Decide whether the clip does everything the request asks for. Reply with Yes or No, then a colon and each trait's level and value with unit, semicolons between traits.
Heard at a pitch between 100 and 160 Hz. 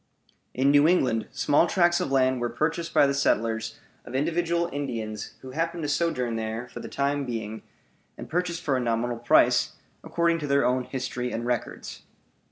Yes: low, 135 Hz